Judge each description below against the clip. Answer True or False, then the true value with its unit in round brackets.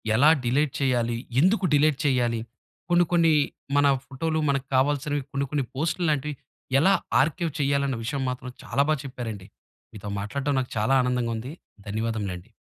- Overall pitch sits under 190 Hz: True (135 Hz)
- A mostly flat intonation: False (3.6 semitones)